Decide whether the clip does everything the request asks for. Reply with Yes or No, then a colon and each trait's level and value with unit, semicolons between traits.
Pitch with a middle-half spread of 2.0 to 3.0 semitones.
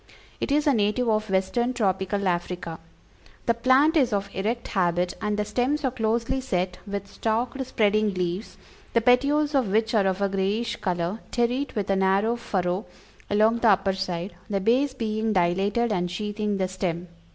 No: average, 3.8 semitones